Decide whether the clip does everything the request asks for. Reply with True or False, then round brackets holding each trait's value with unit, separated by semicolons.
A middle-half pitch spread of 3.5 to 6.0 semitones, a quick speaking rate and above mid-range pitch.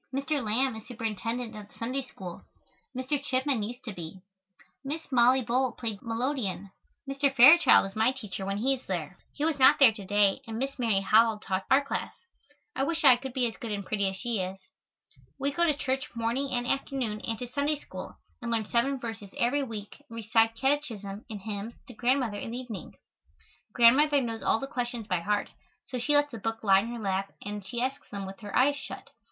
True (4.2 semitones; 215 wpm; 235 Hz)